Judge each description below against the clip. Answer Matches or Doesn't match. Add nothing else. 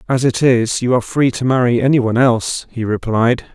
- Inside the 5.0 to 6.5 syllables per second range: Matches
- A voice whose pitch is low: Matches